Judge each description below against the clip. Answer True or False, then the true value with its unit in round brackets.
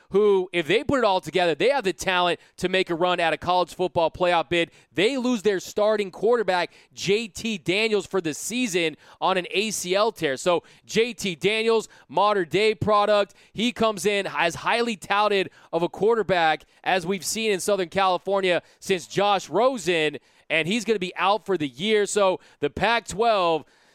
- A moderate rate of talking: True (180 wpm)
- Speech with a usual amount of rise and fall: True (3.3 semitones)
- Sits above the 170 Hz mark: True (190 Hz)